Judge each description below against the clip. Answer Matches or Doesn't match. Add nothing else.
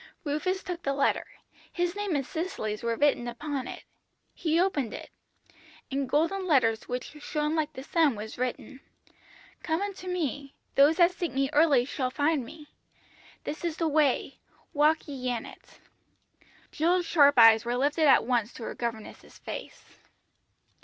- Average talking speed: Matches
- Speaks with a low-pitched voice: Doesn't match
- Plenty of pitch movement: Doesn't match